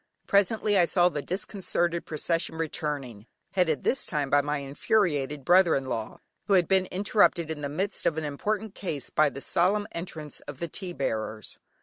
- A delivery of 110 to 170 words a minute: No, average, 180 wpm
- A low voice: No, medium, 165 Hz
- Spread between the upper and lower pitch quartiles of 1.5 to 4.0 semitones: No, average, 4.6 semitones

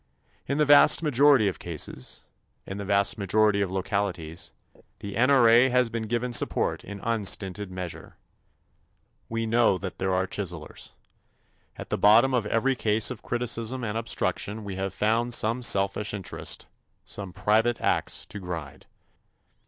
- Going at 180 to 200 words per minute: No, average, 145 wpm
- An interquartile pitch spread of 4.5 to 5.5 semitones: No, average, 3.5 semitones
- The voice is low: Yes, low, 105 Hz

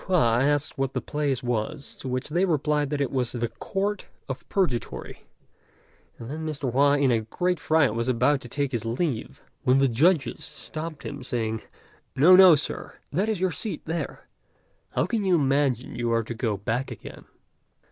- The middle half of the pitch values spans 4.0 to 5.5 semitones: Yes, average, 4.6 semitones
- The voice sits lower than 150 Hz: Yes, medium, 140 Hz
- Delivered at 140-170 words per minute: No, average, 185 wpm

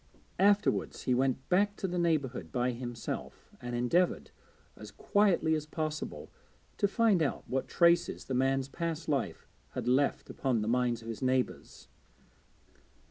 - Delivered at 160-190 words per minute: No, average, 145 wpm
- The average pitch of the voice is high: No, low, 135 Hz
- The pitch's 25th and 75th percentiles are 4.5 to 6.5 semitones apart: Yes, wide, 5.5 semitones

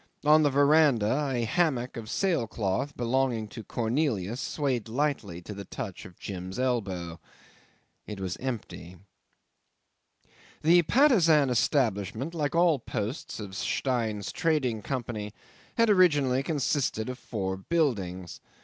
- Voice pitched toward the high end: No, low, 125 Hz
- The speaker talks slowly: Yes, slow, 125 wpm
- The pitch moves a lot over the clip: Yes, wide, 6.1 semitones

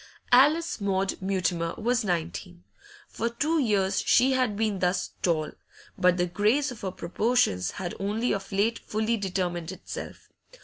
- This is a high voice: Yes, high, 195 Hz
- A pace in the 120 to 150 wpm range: Yes, average, 145 wpm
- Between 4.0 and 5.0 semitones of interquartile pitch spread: Yes, average, 4.5 semitones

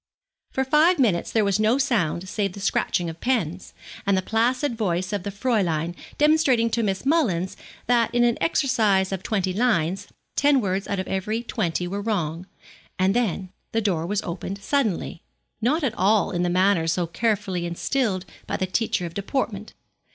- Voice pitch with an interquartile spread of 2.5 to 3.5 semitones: No, average, 4.4 semitones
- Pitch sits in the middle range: No, high, 200 Hz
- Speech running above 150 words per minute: Yes, average, 175 wpm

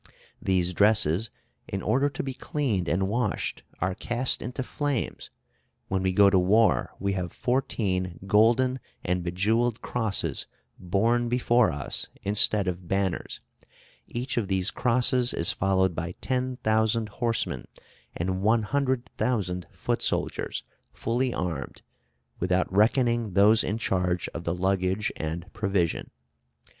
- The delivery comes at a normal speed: No, slow, 125 wpm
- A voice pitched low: Yes, low, 105 Hz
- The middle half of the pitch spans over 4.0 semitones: Yes, average, 4.5 semitones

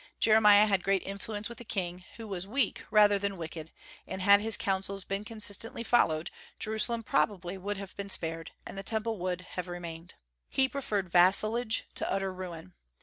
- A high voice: Yes, high, 195 Hz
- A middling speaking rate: Yes, average, 175 wpm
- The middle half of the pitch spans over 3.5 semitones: No, average, 2.9 semitones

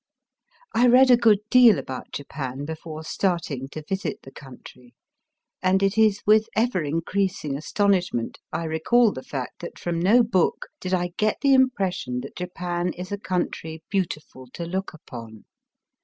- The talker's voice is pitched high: No, medium, 180 Hz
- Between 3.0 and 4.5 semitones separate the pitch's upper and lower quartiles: No, average, 5.2 semitones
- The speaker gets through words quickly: No, average, 155 wpm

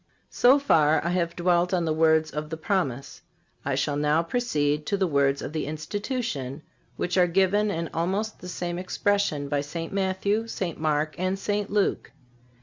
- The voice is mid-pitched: Yes, medium, 170 Hz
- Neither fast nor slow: Yes, average, 175 wpm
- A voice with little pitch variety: No, average, 4.3 semitones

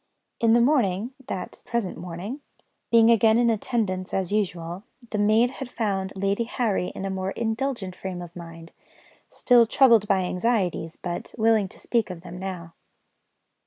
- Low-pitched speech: No, high, 200 Hz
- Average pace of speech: Yes, average, 160 wpm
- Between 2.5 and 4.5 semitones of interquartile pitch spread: Yes, average, 4.2 semitones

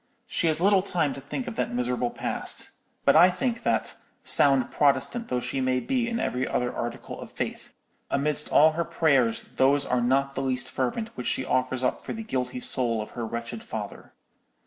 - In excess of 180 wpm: Yes, average, 195 wpm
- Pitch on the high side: No, low, 135 Hz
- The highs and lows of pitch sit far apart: No, average, 4.8 semitones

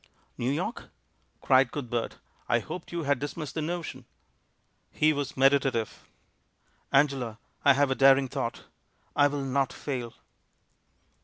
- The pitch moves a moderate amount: No, narrow, 2.0 semitones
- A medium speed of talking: No, slow, 130 wpm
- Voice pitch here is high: No, low, 135 Hz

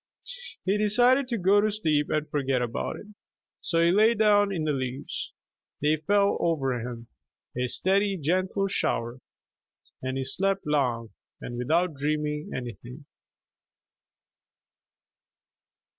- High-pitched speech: No, medium, 155 Hz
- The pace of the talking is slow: Yes, slow, 125 wpm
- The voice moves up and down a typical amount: No, wide, 7.2 semitones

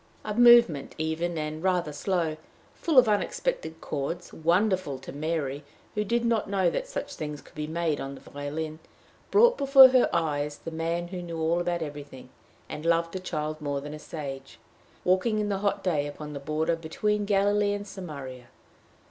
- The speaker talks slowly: No, average, 185 wpm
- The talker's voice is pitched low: No, medium, 165 Hz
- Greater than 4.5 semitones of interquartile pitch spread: Yes, average, 5.0 semitones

